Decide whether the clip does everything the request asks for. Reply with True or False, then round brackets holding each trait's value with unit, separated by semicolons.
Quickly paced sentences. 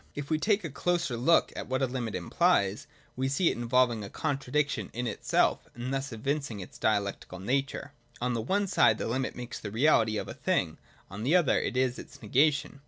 True (210 wpm)